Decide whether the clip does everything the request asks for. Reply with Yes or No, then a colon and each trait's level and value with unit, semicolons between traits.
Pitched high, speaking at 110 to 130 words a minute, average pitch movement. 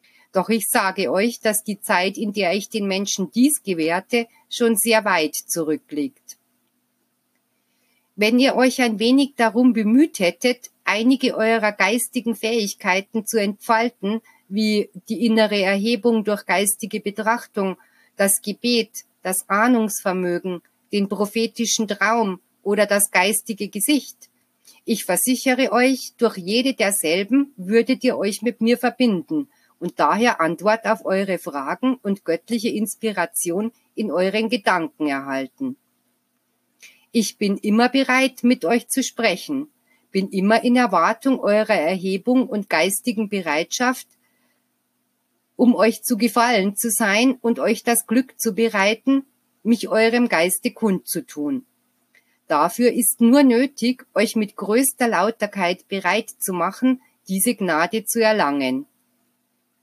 Yes: high, 220 Hz; slow, 125 wpm; average, 3.7 semitones